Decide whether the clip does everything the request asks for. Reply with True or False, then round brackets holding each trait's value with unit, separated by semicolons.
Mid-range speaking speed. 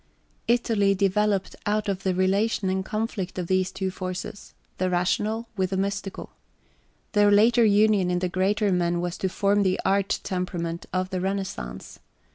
True (165 wpm)